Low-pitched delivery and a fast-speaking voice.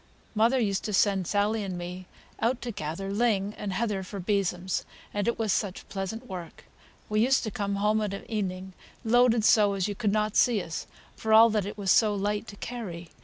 No: high, 205 Hz; fast, 210 wpm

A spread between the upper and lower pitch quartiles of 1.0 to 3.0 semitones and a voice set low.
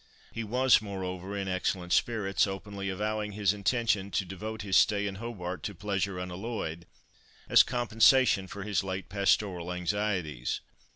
Yes: narrow, 2.4 semitones; low, 100 Hz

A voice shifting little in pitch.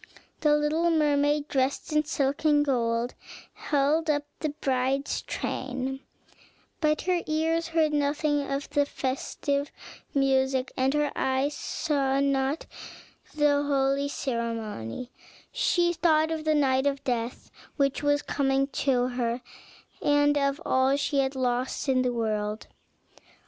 Yes: narrow, 2.2 semitones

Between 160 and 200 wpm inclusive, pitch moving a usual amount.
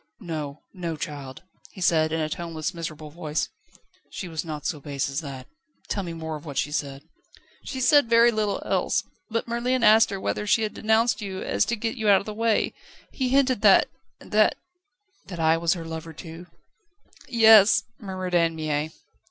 No: average, 195 wpm; wide, 5.8 semitones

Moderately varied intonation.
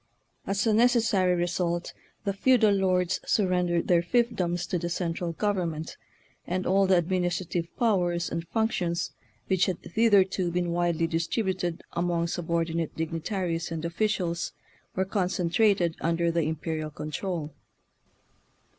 No: narrow, 2.3 semitones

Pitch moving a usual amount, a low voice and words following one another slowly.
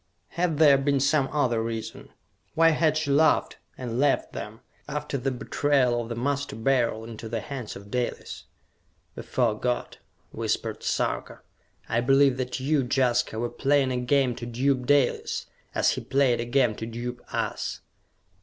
No: average, 3.0 semitones; low, 130 Hz; average, 160 wpm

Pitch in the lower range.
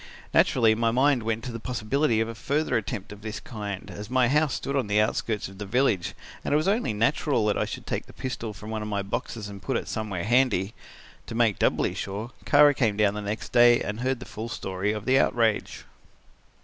Yes: low, 110 Hz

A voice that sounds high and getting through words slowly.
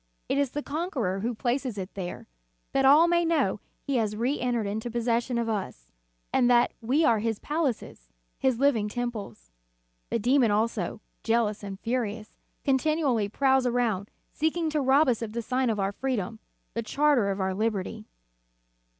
No: high, 235 Hz; average, 165 wpm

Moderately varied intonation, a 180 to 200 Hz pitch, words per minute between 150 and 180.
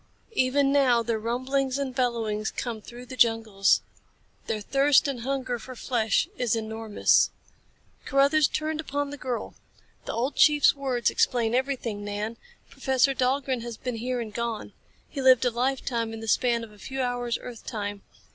No: average, 3.0 semitones; high, 245 Hz; average, 165 wpm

